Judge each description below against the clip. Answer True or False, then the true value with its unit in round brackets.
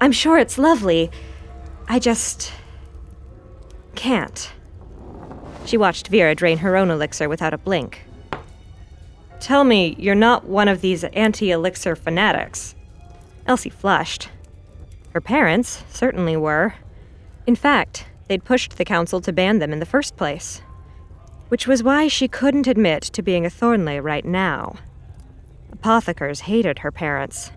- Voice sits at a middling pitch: True (165 Hz)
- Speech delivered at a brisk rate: False (135 wpm)